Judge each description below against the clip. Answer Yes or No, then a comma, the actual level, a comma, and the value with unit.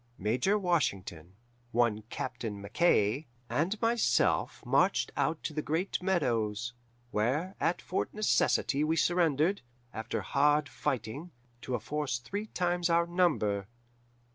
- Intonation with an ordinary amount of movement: No, wide, 7.4 semitones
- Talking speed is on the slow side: Yes, slow, 120 wpm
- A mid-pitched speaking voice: Yes, medium, 150 Hz